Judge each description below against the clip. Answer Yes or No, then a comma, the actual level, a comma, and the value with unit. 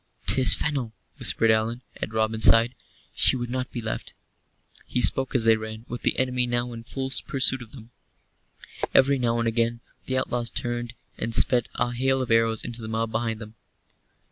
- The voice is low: Yes, low, 120 Hz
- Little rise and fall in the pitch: Yes, narrow, 1.9 semitones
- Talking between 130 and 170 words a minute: No, average, 185 wpm